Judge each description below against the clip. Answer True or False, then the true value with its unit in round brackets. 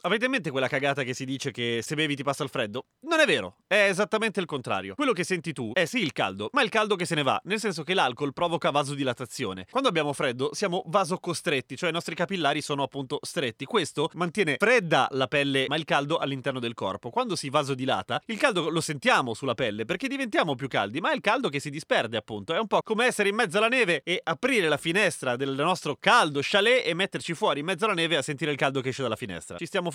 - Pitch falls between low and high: True (160 Hz)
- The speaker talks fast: True (245 wpm)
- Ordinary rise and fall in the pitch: False (6.0 semitones)